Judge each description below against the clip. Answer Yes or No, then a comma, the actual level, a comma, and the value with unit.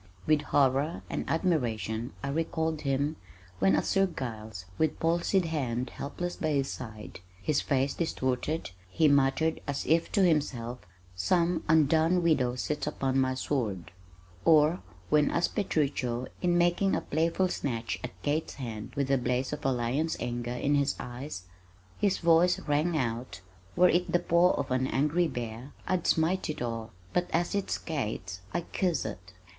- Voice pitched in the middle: Yes, medium, 145 Hz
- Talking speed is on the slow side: No, average, 160 wpm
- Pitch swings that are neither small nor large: Yes, average, 4.9 semitones